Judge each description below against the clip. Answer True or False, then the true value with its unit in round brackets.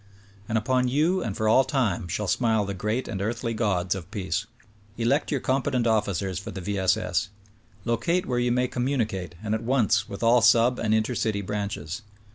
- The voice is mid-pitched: False (110 Hz)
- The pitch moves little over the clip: False (3.7 semitones)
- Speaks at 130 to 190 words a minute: False (200 wpm)